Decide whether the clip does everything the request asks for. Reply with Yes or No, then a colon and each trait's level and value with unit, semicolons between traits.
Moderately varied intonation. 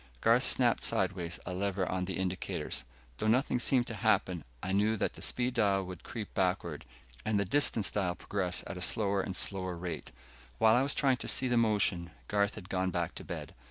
Yes: average, 3.1 semitones